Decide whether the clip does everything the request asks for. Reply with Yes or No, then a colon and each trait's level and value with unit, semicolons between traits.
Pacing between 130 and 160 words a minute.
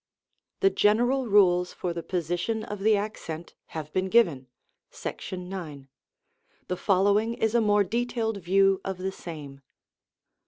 Yes: average, 140 wpm